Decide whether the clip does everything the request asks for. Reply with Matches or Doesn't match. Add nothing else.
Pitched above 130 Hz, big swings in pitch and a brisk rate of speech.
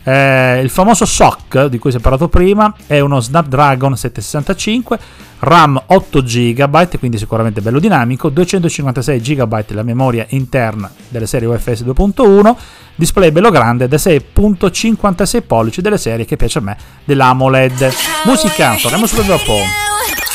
Doesn't match